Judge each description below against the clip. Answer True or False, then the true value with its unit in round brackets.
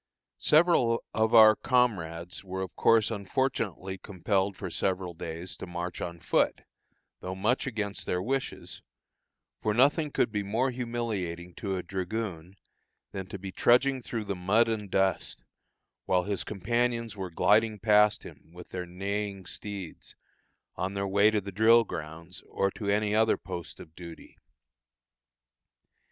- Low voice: True (100 Hz)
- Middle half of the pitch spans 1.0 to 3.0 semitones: False (3.5 semitones)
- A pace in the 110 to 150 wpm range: True (145 wpm)